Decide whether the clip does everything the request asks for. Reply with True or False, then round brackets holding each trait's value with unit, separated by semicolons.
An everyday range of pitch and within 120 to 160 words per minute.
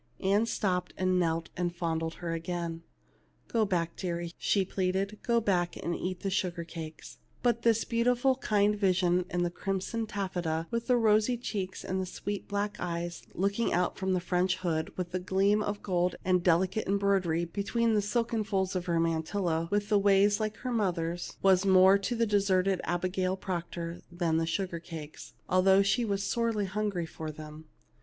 False (3.0 semitones; 180 wpm)